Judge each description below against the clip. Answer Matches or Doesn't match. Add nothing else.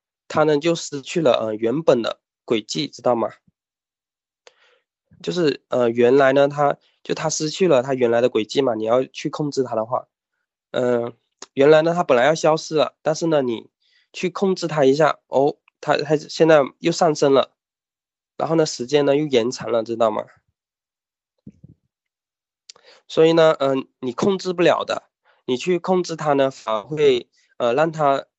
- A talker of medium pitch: Matches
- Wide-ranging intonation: Doesn't match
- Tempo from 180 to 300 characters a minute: Matches